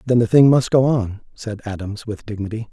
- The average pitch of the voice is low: Yes, low, 110 Hz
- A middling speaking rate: No, fast, 220 wpm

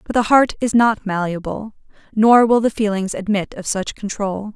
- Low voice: No, high, 210 Hz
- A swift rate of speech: No, average, 185 wpm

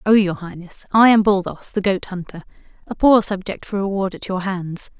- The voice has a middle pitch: No, high, 195 Hz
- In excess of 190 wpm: Yes, fast, 205 wpm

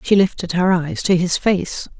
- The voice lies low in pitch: No, medium, 185 Hz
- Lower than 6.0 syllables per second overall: Yes, 4.4 syllables/s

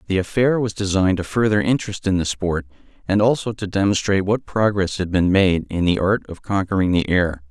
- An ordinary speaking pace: No, fast, 210 wpm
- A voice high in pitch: No, very low, 95 Hz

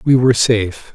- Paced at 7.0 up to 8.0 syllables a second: No, 5.9 syllables/s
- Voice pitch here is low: Yes, low, 115 Hz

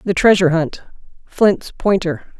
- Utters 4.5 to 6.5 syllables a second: No, 4.3 syllables/s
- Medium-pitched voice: Yes, medium, 180 Hz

